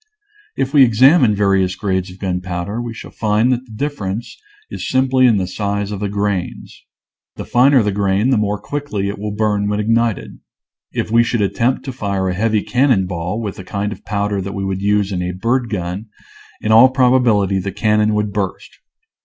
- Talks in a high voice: No, low, 105 Hz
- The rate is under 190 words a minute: No, average, 195 wpm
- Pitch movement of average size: Yes, average, 3.2 semitones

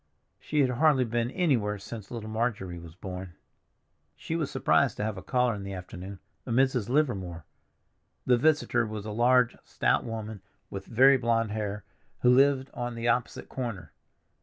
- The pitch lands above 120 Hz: No, low, 115 Hz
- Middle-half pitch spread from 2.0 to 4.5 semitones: Yes, average, 3.8 semitones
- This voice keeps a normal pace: Yes, average, 165 wpm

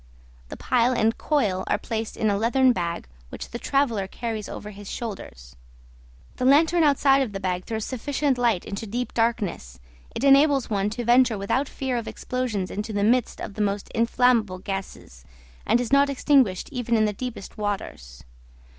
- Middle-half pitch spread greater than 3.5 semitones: Yes, average, 4.1 semitones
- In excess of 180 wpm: No, average, 175 wpm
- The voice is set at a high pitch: Yes, high, 225 Hz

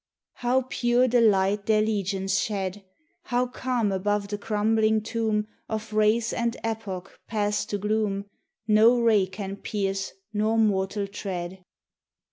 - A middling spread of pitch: No, narrow, 2.1 semitones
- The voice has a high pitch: Yes, high, 210 Hz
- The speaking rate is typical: No, slow, 130 wpm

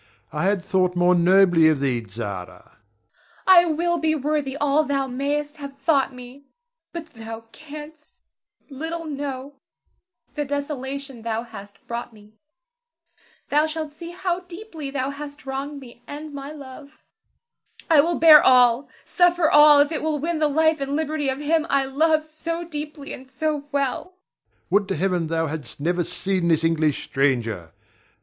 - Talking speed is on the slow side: No, average, 160 wpm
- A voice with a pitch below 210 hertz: No, very high, 280 Hz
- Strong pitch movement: Yes, wide, 5.8 semitones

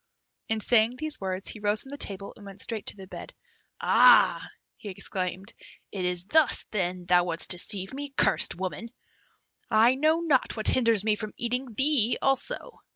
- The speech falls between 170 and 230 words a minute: Yes, average, 175 wpm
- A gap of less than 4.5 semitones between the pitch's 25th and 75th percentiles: No, average, 4.9 semitones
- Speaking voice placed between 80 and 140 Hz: No, high, 215 Hz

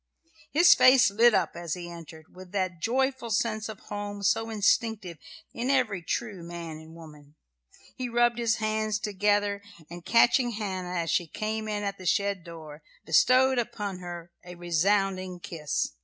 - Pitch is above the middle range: Yes, high, 200 Hz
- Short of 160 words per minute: No, average, 165 wpm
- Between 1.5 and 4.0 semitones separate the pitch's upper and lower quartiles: No, average, 4.4 semitones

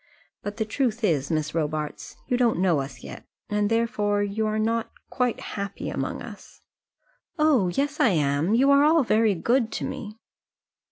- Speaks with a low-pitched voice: No, high, 215 Hz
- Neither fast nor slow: Yes, average, 170 wpm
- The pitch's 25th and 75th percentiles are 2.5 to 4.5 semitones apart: No, average, 5.3 semitones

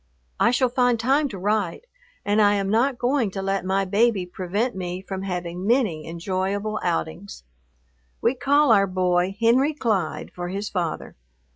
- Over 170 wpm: No, average, 160 wpm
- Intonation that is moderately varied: Yes, average, 4.3 semitones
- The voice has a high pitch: Yes, high, 200 Hz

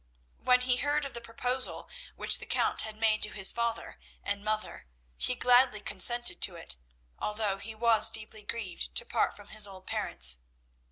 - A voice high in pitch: Yes, high, 220 Hz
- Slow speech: No, average, 175 wpm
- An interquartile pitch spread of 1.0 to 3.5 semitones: Yes, average, 2.7 semitones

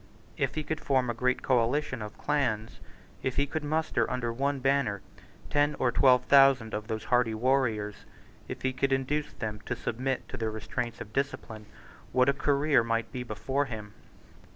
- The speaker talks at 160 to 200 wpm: Yes, average, 175 wpm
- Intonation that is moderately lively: Yes, average, 3.6 semitones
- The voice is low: Yes, low, 125 Hz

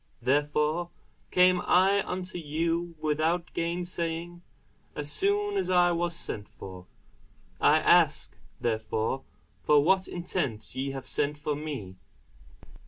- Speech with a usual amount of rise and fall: Yes, average, 3.5 semitones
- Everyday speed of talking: No, slow, 115 wpm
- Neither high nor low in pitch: Yes, medium, 165 Hz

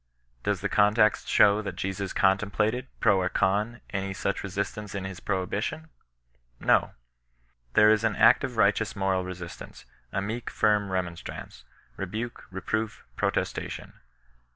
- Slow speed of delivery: Yes, slow, 130 wpm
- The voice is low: Yes, low, 100 Hz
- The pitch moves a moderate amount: No, narrow, 2.0 semitones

